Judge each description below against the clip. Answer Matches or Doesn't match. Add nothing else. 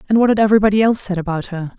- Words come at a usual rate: Doesn't match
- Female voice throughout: Matches